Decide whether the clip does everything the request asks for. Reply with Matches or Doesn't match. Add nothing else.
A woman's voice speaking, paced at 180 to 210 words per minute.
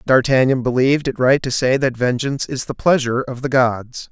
Doesn't match